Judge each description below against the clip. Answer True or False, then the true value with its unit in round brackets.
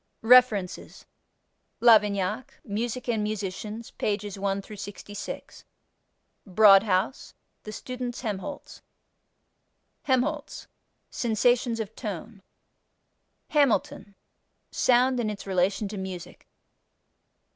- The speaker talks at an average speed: False (80 wpm)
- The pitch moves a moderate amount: True (3.5 semitones)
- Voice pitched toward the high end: True (215 Hz)